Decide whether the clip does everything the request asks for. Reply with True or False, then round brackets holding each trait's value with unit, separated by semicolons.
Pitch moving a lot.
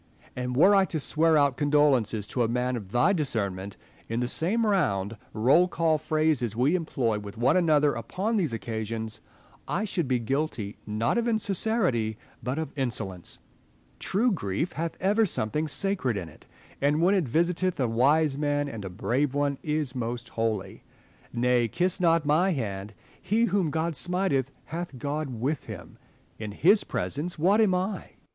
True (6.8 semitones)